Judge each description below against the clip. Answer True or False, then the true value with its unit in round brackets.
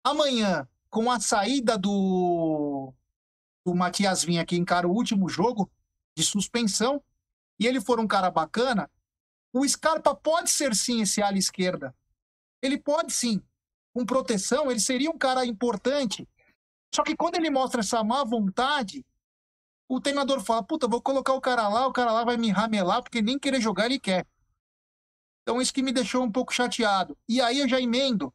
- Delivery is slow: False (170 wpm)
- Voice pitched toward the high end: True (235 Hz)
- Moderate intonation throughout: False (5.9 semitones)